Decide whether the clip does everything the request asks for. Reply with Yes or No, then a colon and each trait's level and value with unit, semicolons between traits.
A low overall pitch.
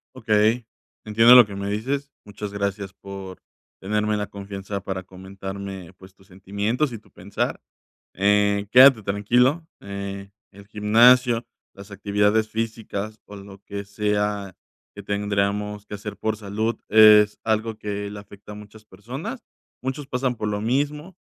Yes: low, 105 Hz